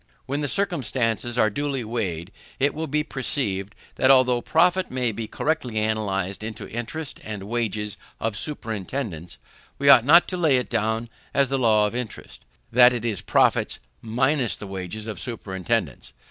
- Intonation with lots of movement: No, average, 4.2 semitones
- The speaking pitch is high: No, low, 120 Hz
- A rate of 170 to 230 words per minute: No, average, 160 wpm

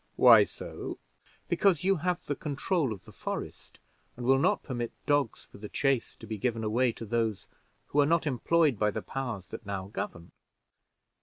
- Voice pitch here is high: No, low, 125 Hz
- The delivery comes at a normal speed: Yes, average, 180 wpm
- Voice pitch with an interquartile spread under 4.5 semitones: No, average, 5.1 semitones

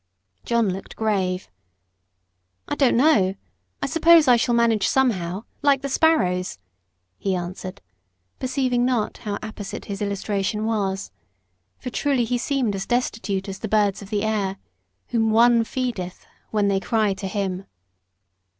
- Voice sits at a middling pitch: No, high, 215 Hz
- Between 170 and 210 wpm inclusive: No, average, 140 wpm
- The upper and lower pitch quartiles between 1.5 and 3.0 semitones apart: No, average, 3.9 semitones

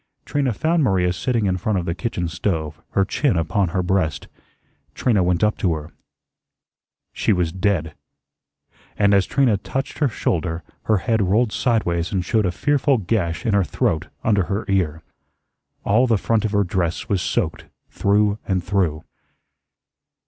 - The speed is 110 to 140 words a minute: No, average, 165 wpm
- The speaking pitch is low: Yes, very low, 95 Hz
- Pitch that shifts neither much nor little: Yes, average, 4.0 semitones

